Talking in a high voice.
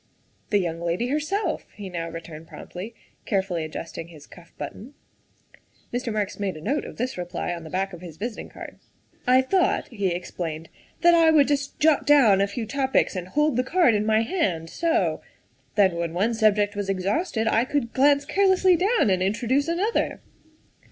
Yes: high, 215 Hz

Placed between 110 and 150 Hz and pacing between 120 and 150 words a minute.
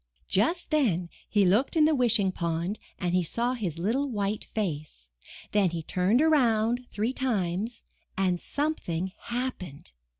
No: high, 210 Hz; average, 140 wpm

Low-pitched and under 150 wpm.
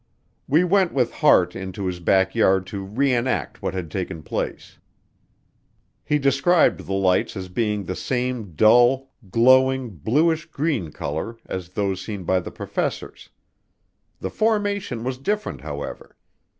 Yes: low, 115 Hz; average, 140 wpm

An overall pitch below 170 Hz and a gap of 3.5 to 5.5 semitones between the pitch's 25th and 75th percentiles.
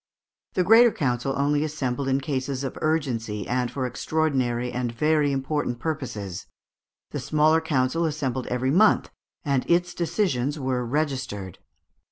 Yes: low, 135 Hz; average, 3.8 semitones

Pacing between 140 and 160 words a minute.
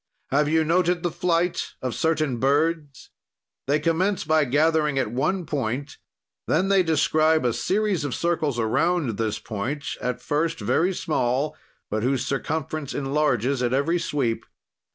Yes: average, 145 wpm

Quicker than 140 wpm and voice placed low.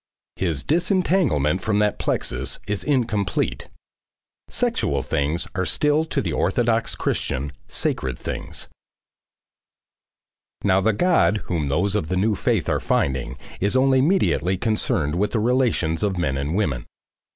No: slow, 135 wpm; low, 100 Hz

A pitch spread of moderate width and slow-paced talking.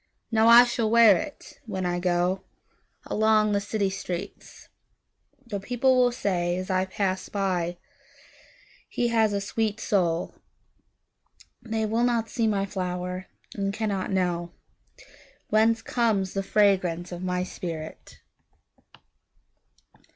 Yes: average, 3.6 semitones; slow, 100 wpm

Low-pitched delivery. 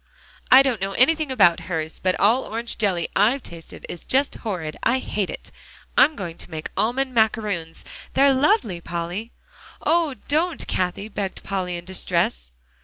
No: high, 205 Hz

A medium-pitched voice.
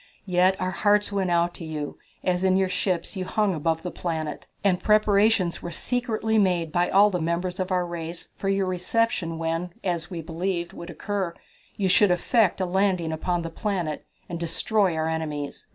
Yes: medium, 180 Hz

